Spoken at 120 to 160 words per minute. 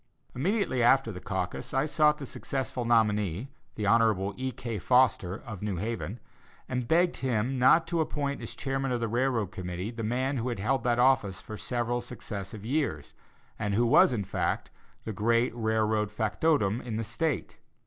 No: average, 170 wpm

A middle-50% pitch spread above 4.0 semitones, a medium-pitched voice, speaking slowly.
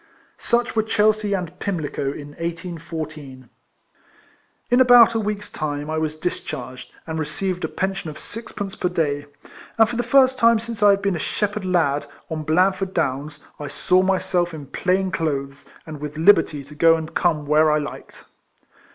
No: average, 5.0 semitones; medium, 170 Hz; average, 170 wpm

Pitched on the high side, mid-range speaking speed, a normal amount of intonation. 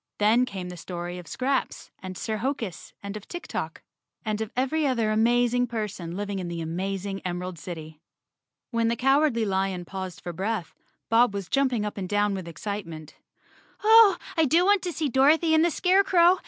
No: high, 215 Hz; average, 185 wpm; wide, 6.4 semitones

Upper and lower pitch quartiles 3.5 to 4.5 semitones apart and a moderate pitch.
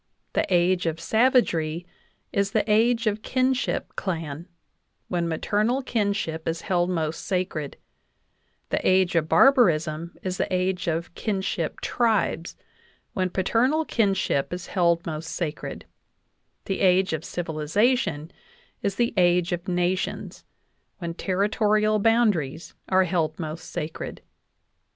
Yes: average, 4.1 semitones; medium, 180 Hz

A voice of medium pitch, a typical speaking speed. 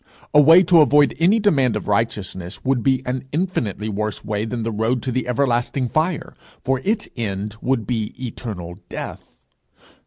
No: low, 125 Hz; average, 165 wpm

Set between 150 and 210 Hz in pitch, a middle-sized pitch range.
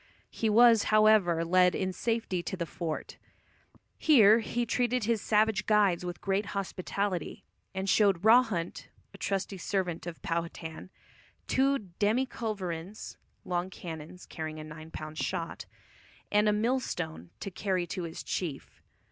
Yes: high, 190 Hz; average, 4.1 semitones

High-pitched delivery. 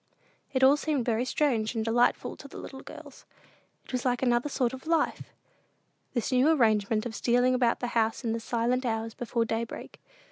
Yes: high, 245 Hz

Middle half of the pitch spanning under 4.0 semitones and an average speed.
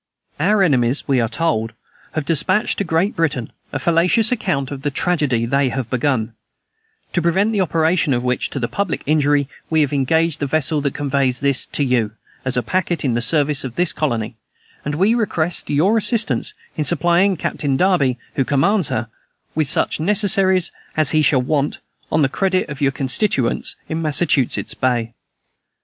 No: average, 4.6 semitones; average, 175 wpm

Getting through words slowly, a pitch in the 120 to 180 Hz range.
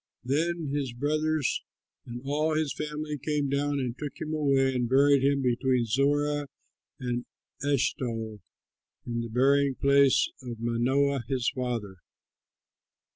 Yes: slow, 130 wpm; low, 135 Hz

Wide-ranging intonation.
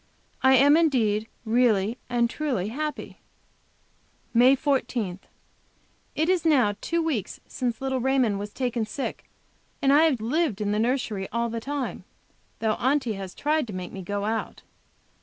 No: average, 4.6 semitones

